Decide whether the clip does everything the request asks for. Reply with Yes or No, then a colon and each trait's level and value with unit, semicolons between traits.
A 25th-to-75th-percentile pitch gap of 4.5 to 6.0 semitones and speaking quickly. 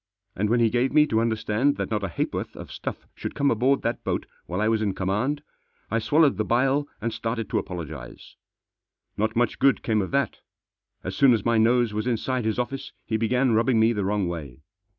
No: average, 3.1 semitones; fast, 215 wpm